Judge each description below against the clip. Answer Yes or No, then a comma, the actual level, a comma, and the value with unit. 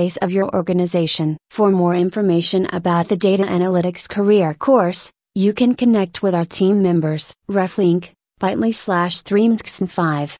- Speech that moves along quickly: No, slow, 135 wpm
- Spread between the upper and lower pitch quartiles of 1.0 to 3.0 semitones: Yes, narrow, 2.4 semitones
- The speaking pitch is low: No, medium, 185 Hz